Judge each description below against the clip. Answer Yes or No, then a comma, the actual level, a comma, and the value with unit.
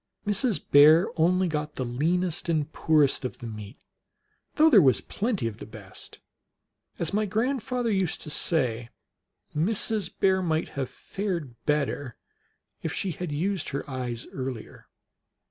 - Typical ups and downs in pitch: No, wide, 6.4 semitones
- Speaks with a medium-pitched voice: Yes, medium, 160 Hz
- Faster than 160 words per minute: No, average, 145 wpm